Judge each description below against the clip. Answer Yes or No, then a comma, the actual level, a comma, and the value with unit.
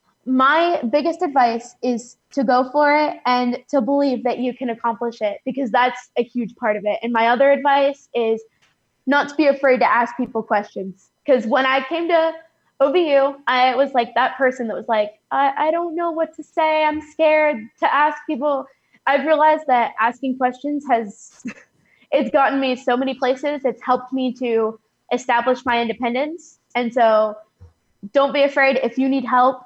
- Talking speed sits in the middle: Yes, average, 180 wpm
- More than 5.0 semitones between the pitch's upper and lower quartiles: No, average, 3.2 semitones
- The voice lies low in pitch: No, very high, 260 Hz